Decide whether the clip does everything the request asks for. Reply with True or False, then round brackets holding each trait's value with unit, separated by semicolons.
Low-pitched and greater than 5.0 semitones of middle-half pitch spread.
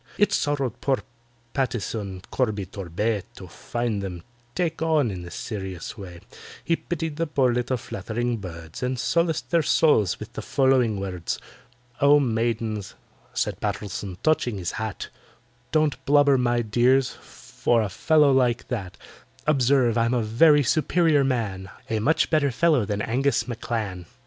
True (120 Hz; 5.5 semitones)